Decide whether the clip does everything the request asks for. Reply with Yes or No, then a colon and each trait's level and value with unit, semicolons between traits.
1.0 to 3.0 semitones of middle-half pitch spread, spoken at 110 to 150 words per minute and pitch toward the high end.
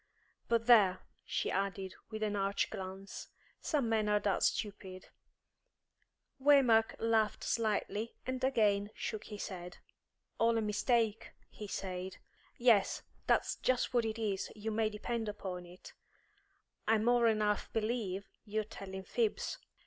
Yes: narrow, 2.6 semitones; slow, 135 wpm; high, 215 Hz